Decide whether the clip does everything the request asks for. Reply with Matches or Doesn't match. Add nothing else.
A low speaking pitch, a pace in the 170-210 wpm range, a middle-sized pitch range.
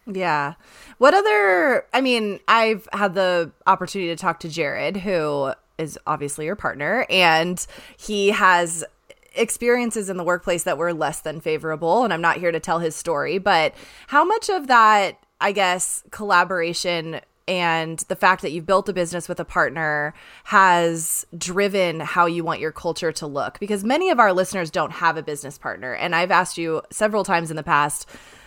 Doesn't match